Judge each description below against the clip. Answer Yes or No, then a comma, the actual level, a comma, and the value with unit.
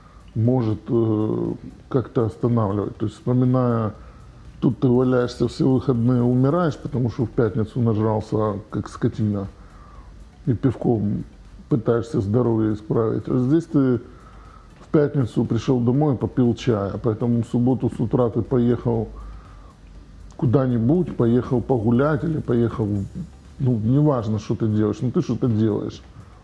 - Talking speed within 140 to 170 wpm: No, average, 125 wpm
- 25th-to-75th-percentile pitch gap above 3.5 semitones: No, average, 2.8 semitones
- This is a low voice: Yes, low, 120 Hz